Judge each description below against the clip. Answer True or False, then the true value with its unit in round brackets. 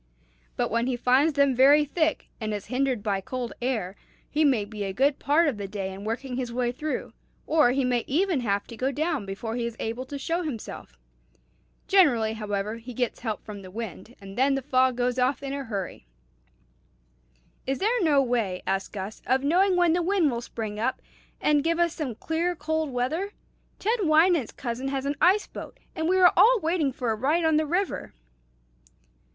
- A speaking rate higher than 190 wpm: True (200 wpm)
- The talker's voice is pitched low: False (260 Hz)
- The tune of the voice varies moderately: False (5.7 semitones)